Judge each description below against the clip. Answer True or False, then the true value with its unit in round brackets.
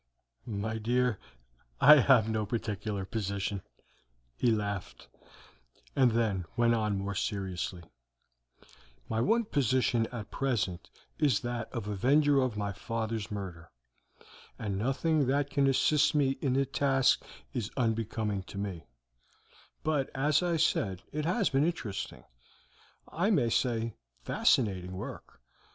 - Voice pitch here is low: True (115 Hz)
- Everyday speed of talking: False (130 wpm)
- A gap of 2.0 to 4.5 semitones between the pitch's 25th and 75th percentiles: False (5.1 semitones)